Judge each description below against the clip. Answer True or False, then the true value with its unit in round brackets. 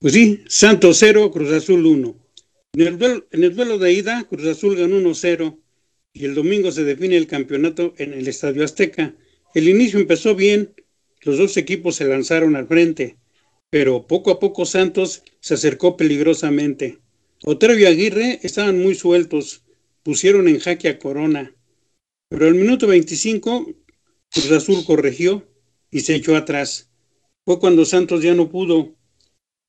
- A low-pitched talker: False (175 Hz)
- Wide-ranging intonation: False (4.8 semitones)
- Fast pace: False (150 wpm)